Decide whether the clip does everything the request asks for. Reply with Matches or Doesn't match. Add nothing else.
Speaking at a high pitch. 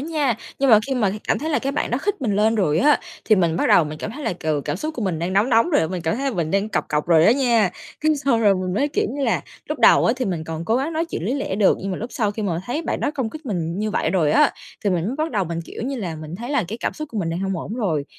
Matches